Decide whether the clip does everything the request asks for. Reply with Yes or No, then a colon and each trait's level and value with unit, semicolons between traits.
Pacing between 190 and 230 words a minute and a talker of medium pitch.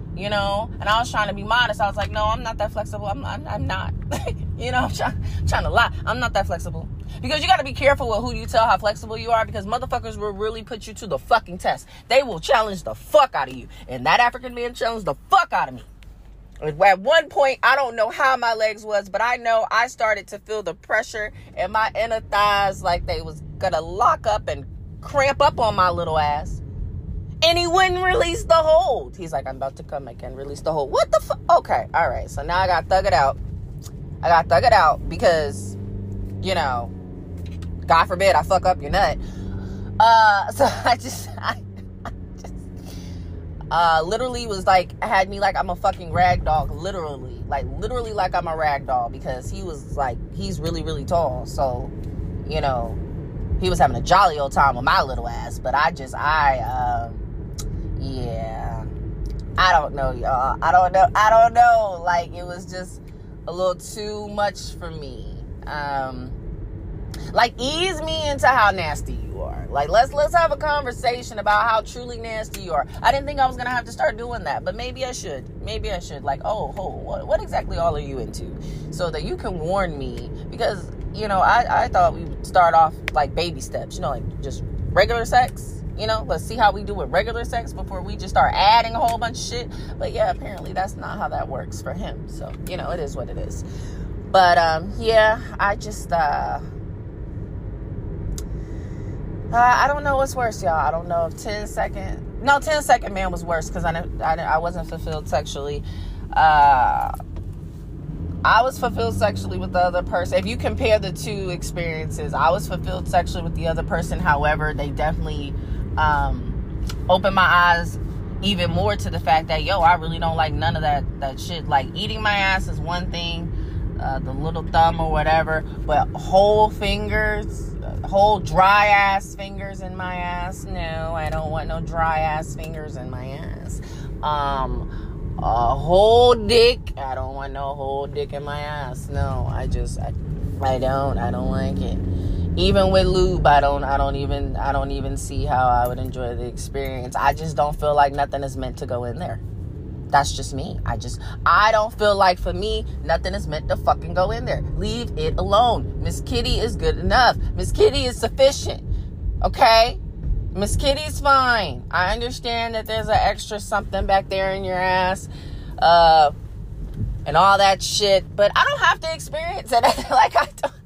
Yes: average, 200 wpm; medium, 155 Hz